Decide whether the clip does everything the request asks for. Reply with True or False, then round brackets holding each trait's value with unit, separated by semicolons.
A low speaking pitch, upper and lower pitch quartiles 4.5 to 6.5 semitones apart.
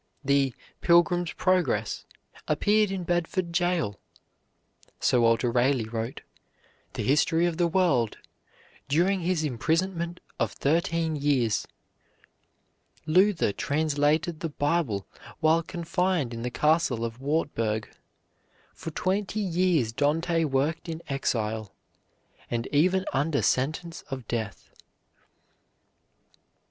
False (155 Hz; 5.1 semitones)